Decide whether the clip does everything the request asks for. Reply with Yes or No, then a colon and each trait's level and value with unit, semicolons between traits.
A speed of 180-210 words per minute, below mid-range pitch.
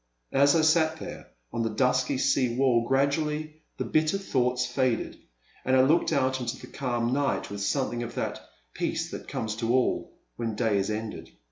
Yes: average, 190 wpm; low, 130 Hz